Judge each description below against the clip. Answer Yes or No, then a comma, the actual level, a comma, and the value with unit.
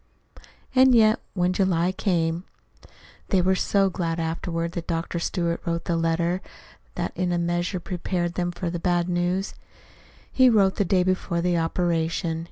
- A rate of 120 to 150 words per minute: No, average, 160 wpm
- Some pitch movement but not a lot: No, narrow, 1.8 semitones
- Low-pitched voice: No, medium, 175 Hz